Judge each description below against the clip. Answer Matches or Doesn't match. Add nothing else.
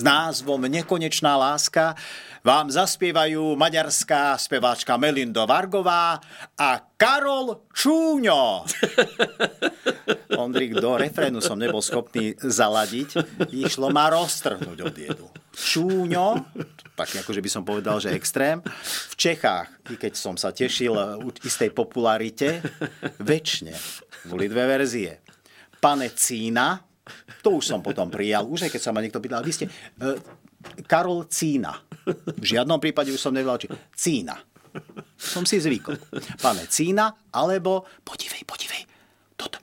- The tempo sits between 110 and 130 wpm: Matches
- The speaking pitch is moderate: Matches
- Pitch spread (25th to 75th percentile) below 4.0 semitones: Doesn't match